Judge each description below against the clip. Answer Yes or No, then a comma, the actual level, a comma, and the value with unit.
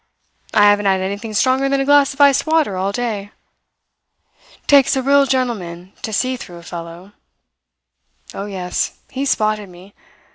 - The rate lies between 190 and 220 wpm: No, average, 155 wpm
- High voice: Yes, high, 215 Hz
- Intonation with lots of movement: Yes, wide, 6.0 semitones